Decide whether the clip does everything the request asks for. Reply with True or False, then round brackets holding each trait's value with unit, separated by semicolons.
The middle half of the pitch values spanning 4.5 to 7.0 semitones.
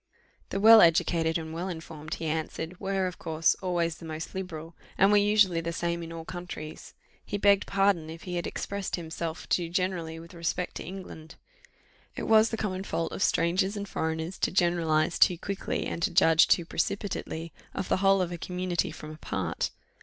False (2.8 semitones)